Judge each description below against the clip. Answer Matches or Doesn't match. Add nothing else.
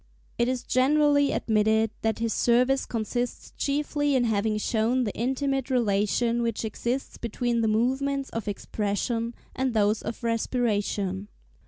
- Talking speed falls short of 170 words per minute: Matches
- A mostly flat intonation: Doesn't match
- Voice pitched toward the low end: Doesn't match